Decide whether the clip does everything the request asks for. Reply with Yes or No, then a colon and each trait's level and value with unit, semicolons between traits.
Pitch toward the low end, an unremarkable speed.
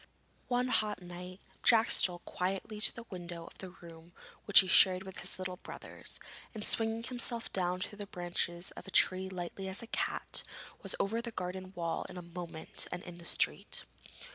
No: medium, 185 Hz; average, 190 wpm